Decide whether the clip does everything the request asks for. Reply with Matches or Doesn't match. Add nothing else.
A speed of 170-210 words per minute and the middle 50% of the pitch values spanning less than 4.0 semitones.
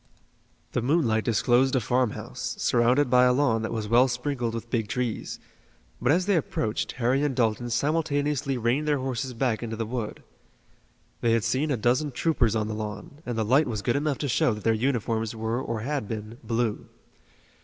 Matches